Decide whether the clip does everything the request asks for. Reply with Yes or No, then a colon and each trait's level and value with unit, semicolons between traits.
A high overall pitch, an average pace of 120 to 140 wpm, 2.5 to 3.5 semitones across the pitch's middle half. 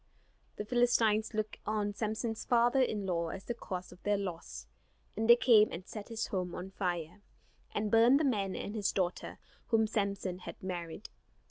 No: high, 210 Hz; average, 175 wpm; average, 3.2 semitones